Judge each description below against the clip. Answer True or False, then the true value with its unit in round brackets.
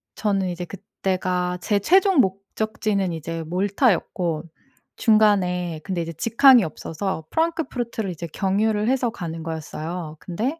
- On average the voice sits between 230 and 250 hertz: False (190 Hz)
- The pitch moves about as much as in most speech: True (4.2 semitones)